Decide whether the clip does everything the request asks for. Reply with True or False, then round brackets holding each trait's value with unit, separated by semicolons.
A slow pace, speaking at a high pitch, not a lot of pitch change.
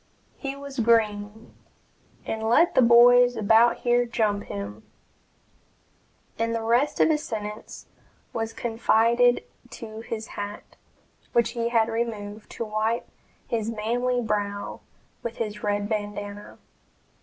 True (120 wpm; 225 Hz; 2.1 semitones)